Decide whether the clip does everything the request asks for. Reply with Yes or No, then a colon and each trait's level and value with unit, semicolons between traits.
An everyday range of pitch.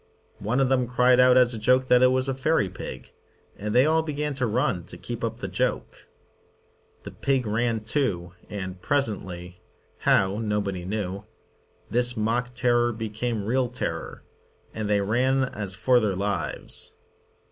Yes: average, 3.9 semitones